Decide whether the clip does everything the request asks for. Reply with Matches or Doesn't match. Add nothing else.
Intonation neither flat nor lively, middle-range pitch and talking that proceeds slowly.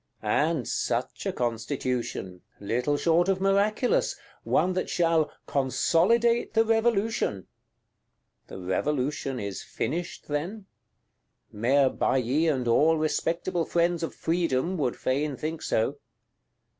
Doesn't match